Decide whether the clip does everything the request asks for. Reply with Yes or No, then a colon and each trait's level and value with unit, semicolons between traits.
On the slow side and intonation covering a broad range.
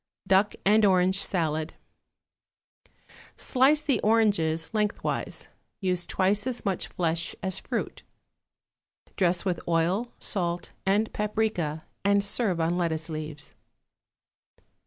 No: slow, 105 wpm; average, 4.0 semitones